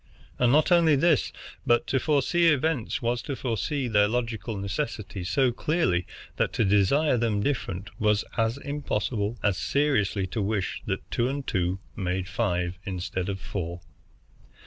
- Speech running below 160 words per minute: Yes, average, 150 wpm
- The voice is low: Yes, low, 115 Hz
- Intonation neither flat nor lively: No, wide, 6.1 semitones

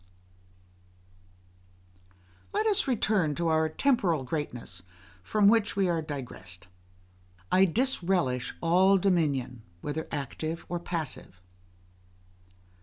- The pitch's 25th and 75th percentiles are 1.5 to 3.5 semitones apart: No, average, 5.2 semitones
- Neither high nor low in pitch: Yes, medium, 165 Hz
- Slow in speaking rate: Yes, slow, 95 wpm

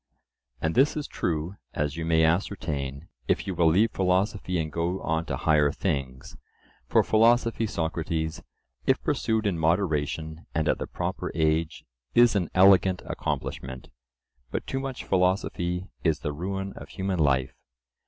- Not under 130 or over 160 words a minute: Yes, average, 150 wpm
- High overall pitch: No, very low, 85 Hz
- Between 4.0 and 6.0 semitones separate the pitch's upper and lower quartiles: No, average, 3.6 semitones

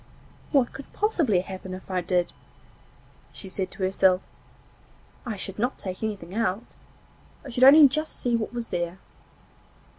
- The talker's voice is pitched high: Yes, high, 200 Hz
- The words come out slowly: No, average, 150 wpm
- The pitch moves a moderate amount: Yes, average, 4.9 semitones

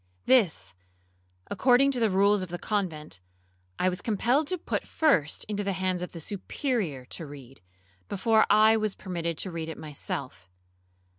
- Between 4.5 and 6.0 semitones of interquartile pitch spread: Yes, average, 5.2 semitones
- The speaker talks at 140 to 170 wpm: Yes, average, 160 wpm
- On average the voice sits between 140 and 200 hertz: Yes, high, 190 Hz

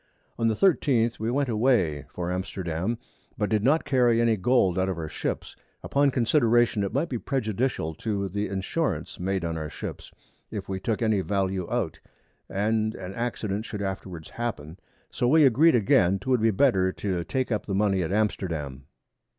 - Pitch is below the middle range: Yes, low, 105 Hz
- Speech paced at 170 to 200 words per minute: Yes, average, 175 wpm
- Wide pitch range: No, average, 4.2 semitones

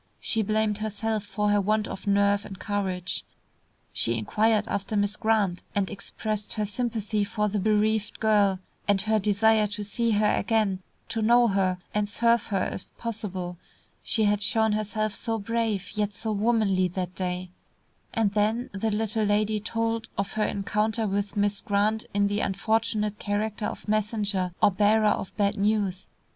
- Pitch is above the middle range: Yes, high, 210 Hz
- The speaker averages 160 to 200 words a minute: Yes, average, 165 wpm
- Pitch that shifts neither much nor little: No, narrow, 1.5 semitones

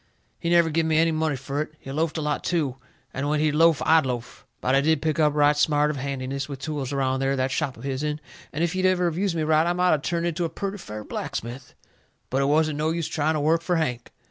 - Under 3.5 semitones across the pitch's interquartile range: Yes, average, 2.9 semitones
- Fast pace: Yes, fast, 265 wpm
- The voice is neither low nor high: Yes, medium, 150 Hz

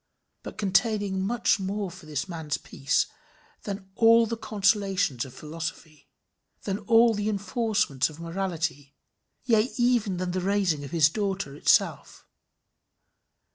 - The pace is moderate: No, slow, 125 wpm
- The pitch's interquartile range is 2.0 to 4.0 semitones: No, average, 4.6 semitones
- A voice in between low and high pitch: No, high, 195 Hz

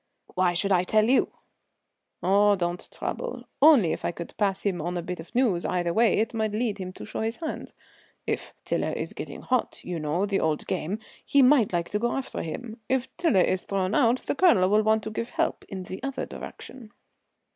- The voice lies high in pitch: Yes, high, 205 Hz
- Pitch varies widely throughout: No, average, 4.8 semitones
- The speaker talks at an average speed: No, fast, 210 wpm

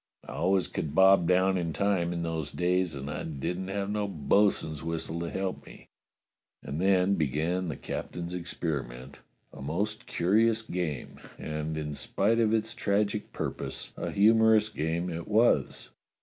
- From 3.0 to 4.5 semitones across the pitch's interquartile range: Yes, average, 4.2 semitones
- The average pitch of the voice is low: Yes, very low, 90 Hz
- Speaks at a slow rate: No, average, 155 wpm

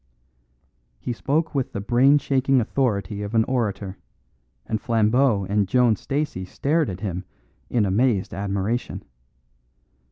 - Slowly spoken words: Yes, slow, 125 wpm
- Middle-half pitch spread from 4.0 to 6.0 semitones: Yes, average, 4.8 semitones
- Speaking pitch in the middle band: No, low, 115 Hz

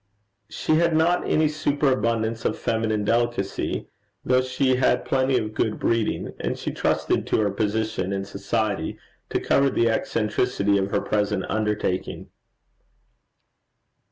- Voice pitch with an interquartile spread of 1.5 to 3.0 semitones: No, average, 3.6 semitones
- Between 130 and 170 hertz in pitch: No, low, 115 Hz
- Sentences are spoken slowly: Yes, slow, 130 wpm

